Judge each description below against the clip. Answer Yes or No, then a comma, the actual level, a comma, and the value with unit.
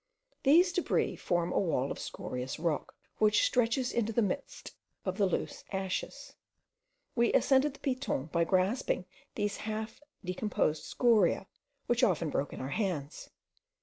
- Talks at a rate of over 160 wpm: No, average, 145 wpm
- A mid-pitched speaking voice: No, high, 205 Hz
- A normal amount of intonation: No, wide, 6.0 semitones